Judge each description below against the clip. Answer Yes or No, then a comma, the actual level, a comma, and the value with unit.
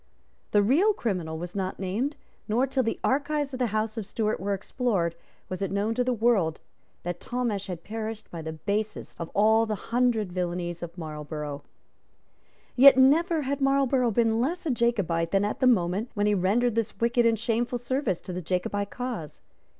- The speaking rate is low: No, average, 185 wpm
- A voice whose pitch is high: Yes, high, 215 Hz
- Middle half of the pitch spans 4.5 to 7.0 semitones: Yes, average, 5.1 semitones